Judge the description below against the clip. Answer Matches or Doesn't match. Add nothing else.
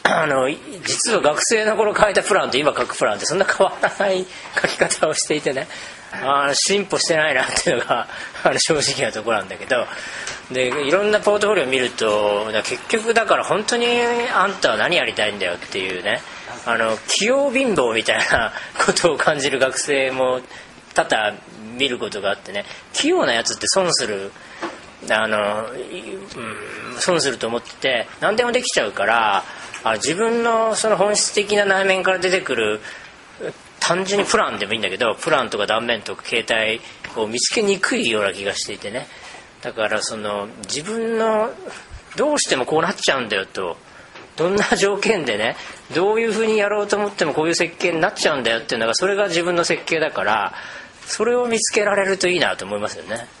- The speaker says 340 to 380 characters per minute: Matches